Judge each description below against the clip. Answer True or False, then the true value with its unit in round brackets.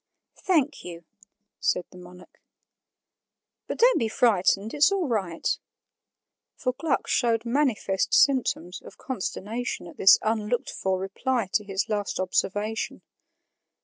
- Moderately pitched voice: False (215 Hz)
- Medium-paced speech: False (120 wpm)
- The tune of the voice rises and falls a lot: False (4.9 semitones)